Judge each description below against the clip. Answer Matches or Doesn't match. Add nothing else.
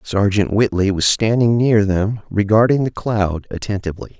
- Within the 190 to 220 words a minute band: Doesn't match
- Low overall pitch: Matches